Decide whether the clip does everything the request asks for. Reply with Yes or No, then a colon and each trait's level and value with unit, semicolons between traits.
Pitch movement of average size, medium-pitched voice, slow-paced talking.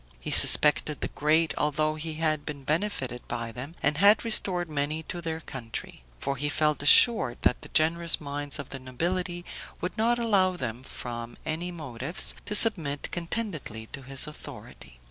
No: average, 4.4 semitones; medium, 155 Hz; average, 165 wpm